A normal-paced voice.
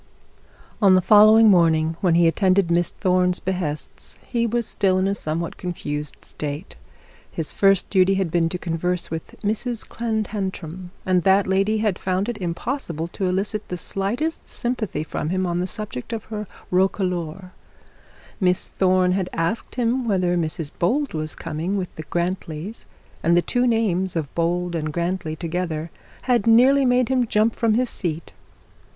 Yes: average, 160 wpm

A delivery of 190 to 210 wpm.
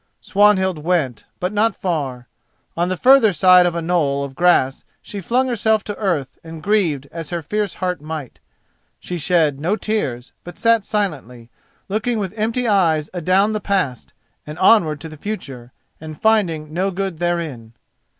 No: average, 165 wpm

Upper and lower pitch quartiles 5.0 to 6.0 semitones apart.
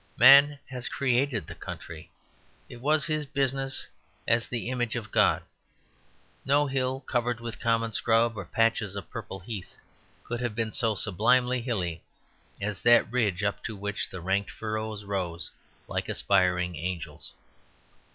No: average, 3.8 semitones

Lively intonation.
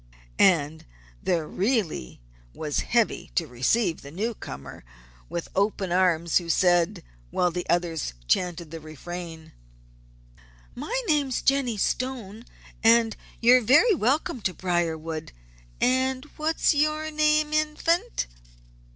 Yes: wide, 7.8 semitones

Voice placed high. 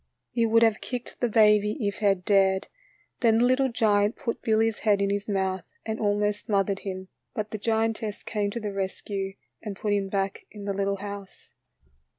Yes: high, 205 Hz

